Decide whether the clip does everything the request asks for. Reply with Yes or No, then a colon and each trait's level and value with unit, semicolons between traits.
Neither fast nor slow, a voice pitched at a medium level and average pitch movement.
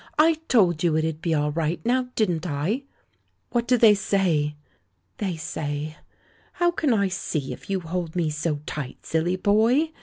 No: average, 170 wpm; medium, 175 Hz; wide, 6.0 semitones